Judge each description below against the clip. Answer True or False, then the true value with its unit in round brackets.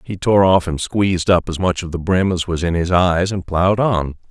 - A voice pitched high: False (90 Hz)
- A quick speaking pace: True (265 wpm)